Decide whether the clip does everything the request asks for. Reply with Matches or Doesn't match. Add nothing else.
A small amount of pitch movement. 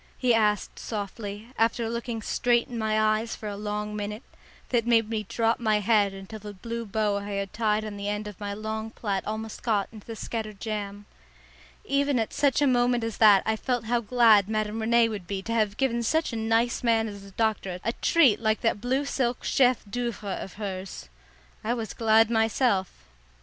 Matches